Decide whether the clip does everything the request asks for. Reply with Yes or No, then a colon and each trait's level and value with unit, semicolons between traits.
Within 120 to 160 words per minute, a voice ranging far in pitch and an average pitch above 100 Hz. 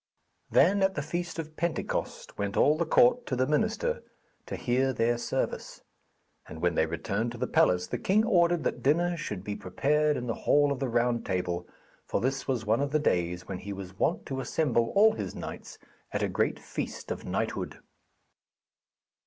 No: average, 190 wpm; wide, 8.2 semitones; low, 135 Hz